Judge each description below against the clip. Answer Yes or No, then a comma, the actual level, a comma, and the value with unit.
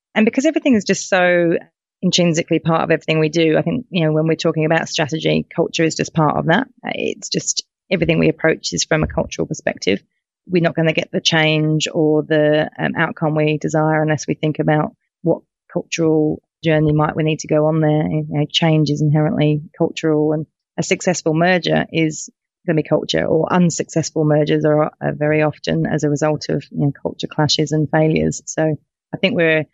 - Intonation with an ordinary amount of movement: No, narrow, 1.4 semitones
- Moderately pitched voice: Yes, medium, 155 Hz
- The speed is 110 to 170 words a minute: No, average, 200 wpm